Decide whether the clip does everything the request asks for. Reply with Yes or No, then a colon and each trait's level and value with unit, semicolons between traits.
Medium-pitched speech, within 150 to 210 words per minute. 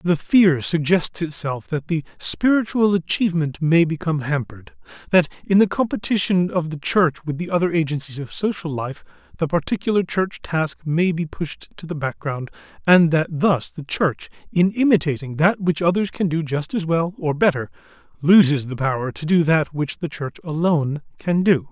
Yes: medium, 165 Hz; average, 175 wpm